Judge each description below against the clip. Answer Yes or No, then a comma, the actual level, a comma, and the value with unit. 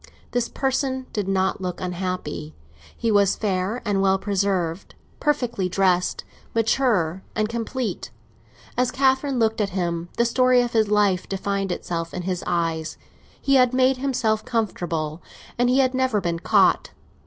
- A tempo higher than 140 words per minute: Yes, average, 150 wpm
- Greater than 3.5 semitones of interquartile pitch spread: Yes, average, 5.2 semitones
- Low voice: No, high, 205 Hz